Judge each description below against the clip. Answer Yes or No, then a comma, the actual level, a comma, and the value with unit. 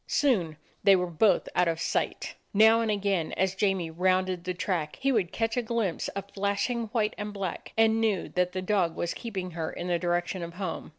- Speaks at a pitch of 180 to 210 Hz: Yes, high, 190 Hz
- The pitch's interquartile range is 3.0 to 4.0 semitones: Yes, average, 3.4 semitones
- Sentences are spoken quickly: Yes, fast, 210 wpm